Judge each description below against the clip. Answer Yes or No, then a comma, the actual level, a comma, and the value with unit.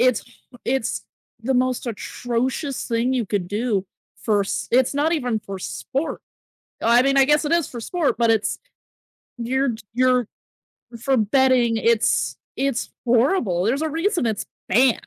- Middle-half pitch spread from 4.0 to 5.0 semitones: No, average, 3.1 semitones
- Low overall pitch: No, very high, 250 Hz